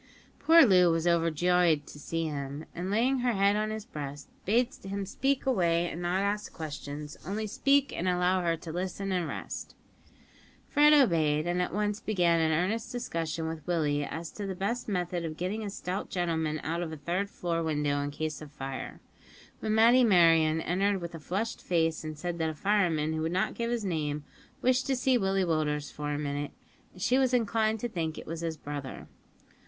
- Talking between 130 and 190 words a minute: No, average, 200 wpm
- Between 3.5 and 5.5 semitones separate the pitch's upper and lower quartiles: Yes, average, 4.7 semitones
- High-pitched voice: No, medium, 175 Hz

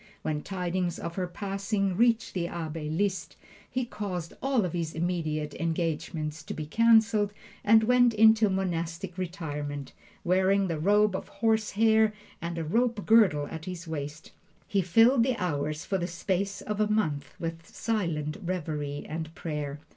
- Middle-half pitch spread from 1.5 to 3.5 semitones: No, average, 4.8 semitones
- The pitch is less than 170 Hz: No, medium, 180 Hz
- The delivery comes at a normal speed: Yes, average, 155 wpm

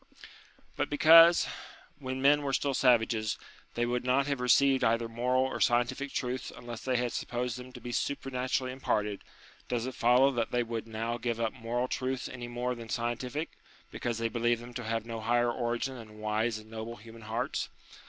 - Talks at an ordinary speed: Yes, average, 190 wpm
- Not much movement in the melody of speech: Yes, narrow, 1.9 semitones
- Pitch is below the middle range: Yes, low, 120 Hz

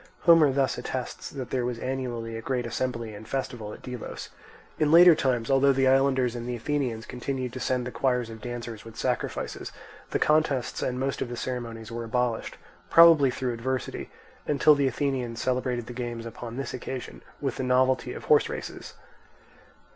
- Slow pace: No, average, 175 wpm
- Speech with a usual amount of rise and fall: No, narrow, 2.2 semitones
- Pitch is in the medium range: No, low, 125 Hz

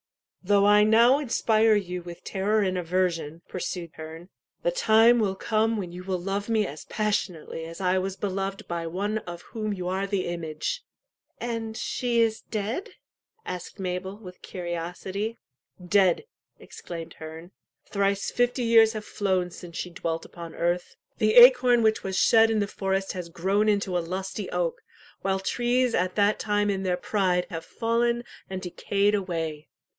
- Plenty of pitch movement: No, average, 3.5 semitones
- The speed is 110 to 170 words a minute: Yes, average, 160 wpm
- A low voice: No, high, 195 Hz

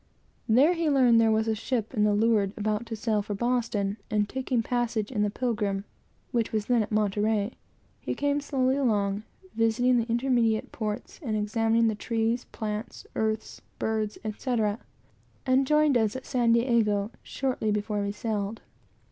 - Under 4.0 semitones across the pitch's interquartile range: Yes, narrow, 2.6 semitones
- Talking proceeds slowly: No, average, 165 wpm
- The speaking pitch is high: Yes, high, 225 Hz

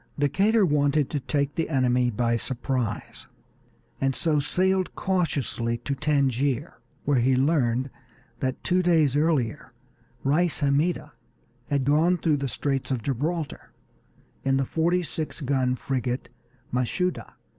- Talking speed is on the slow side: Yes, slow, 125 wpm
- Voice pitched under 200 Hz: Yes, medium, 140 Hz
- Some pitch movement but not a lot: Yes, average, 3.8 semitones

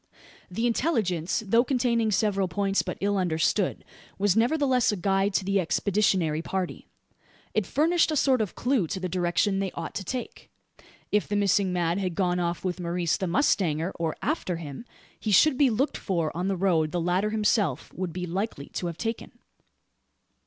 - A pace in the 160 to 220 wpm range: Yes, average, 180 wpm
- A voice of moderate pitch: No, high, 195 Hz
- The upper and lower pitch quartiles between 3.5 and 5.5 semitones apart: Yes, average, 3.9 semitones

